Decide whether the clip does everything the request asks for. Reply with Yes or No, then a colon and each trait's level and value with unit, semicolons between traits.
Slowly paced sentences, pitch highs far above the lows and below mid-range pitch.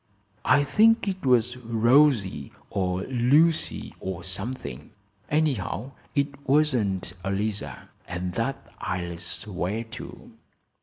Yes: slow, 100 wpm; wide, 6.8 semitones; low, 115 Hz